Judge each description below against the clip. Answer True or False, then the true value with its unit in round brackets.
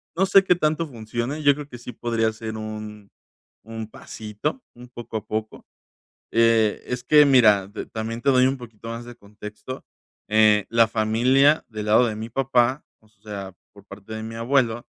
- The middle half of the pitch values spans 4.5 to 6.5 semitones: False (2.8 semitones)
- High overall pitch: False (115 Hz)